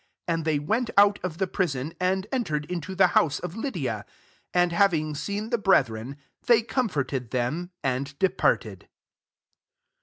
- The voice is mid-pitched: Yes, medium, 175 Hz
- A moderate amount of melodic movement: No, wide, 5.7 semitones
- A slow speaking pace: No, average, 155 wpm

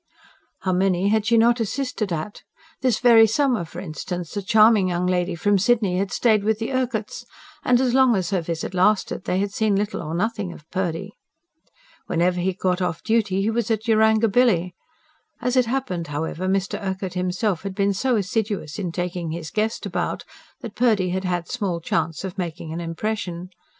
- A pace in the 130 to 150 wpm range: No, average, 185 wpm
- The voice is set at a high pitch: Yes, high, 195 Hz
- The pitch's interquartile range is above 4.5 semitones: No, average, 3.7 semitones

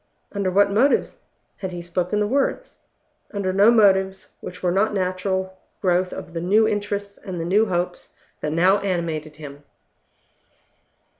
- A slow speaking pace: No, average, 155 wpm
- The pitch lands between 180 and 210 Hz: Yes, high, 190 Hz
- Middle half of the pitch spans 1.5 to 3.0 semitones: Yes, narrow, 2.5 semitones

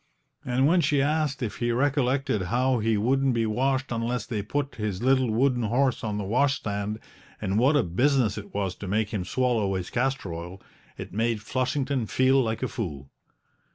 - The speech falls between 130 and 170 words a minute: No, average, 185 wpm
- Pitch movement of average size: Yes, average, 4.2 semitones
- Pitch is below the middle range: Yes, low, 120 Hz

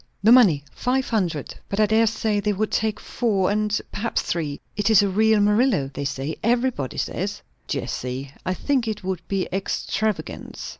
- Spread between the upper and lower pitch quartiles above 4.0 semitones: No, average, 3.4 semitones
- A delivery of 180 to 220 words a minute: No, average, 170 wpm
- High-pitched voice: Yes, high, 210 Hz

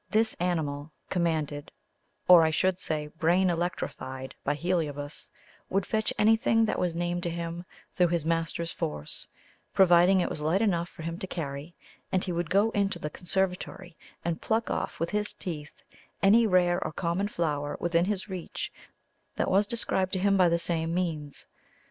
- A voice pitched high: No, medium, 175 Hz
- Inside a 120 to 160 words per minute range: No, average, 170 wpm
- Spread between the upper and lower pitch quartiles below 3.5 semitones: Yes, average, 2.7 semitones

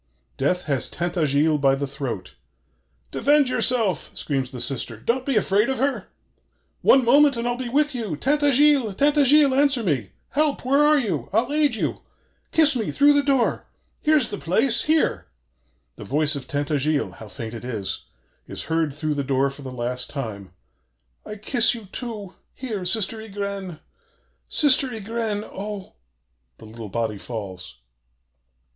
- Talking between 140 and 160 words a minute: Yes, average, 155 wpm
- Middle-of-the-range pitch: No, high, 200 Hz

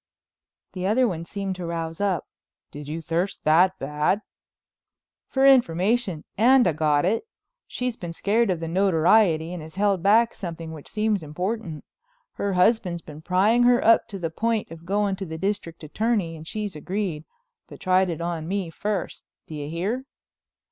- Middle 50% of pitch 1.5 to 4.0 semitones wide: No, average, 4.4 semitones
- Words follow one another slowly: No, average, 170 wpm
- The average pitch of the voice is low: No, medium, 185 Hz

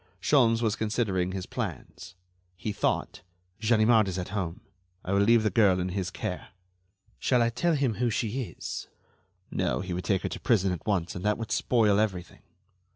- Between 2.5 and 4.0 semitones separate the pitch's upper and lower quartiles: Yes, average, 3.7 semitones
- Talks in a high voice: No, low, 105 Hz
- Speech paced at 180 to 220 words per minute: Yes, average, 185 wpm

